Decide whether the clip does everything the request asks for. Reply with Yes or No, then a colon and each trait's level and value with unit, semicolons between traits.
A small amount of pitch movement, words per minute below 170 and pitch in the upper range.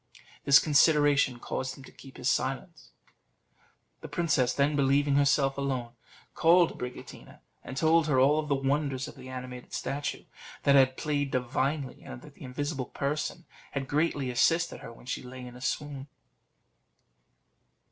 No: narrow, 2.2 semitones; average, 150 wpm; medium, 140 Hz